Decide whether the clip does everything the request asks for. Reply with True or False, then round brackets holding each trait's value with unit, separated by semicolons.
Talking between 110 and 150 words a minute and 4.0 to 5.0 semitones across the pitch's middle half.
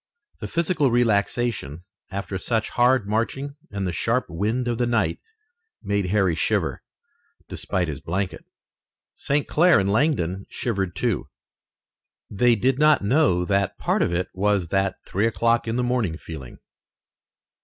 True (145 wpm; 4.5 semitones)